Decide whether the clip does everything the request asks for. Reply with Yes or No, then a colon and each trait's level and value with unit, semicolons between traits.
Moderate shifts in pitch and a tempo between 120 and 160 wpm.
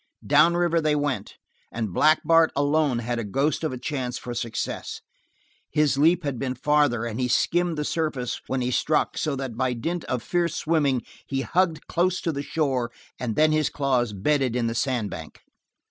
No: average, 4.1 semitones; average, 190 wpm